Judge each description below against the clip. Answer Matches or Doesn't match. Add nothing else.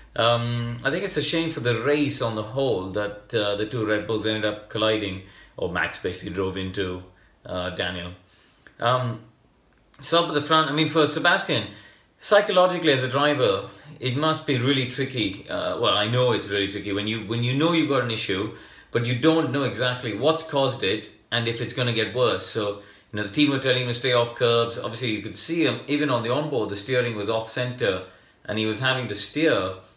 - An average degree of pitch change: Matches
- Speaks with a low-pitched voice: Matches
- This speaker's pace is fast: Matches